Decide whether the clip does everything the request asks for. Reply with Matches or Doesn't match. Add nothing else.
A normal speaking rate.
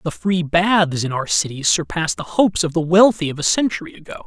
Doesn't match